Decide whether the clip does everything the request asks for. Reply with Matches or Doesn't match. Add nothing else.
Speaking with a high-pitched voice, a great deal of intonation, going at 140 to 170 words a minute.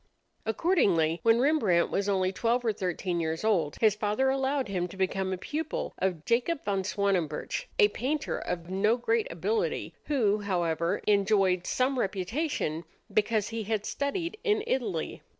Matches